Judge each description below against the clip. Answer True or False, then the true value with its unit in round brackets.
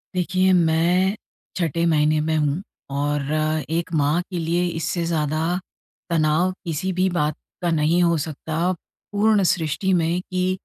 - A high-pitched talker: False (170 Hz)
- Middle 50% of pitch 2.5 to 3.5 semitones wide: True (2.8 semitones)